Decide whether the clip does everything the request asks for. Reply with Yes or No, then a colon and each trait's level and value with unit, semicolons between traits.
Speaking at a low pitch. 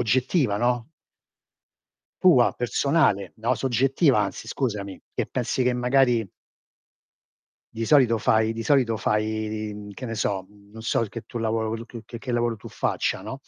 Yes: low, 115 Hz